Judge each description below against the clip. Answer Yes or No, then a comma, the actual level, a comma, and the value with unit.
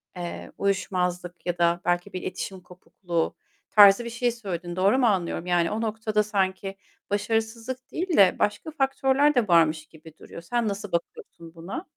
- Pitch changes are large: No, average, 4.2 semitones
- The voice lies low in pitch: No, high, 195 Hz